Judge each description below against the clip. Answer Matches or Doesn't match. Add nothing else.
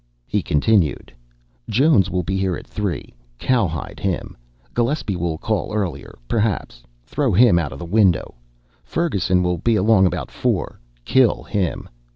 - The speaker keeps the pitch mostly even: Doesn't match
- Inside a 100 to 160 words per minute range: Matches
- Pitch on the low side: Matches